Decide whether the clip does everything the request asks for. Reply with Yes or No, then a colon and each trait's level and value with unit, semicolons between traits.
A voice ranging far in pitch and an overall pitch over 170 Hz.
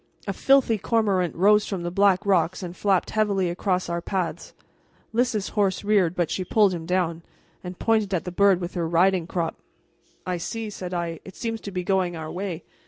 No: average, 2.7 semitones; medium, 185 Hz